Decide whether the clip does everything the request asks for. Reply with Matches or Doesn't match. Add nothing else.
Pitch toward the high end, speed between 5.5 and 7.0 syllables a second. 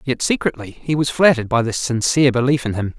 Doesn't match